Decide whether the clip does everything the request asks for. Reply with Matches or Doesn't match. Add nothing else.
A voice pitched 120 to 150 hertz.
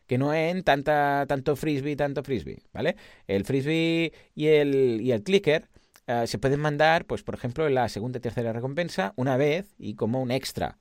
Matches